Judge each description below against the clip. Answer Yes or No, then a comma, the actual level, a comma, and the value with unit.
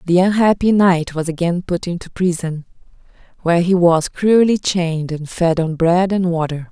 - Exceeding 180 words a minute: No, average, 170 wpm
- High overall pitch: No, medium, 175 Hz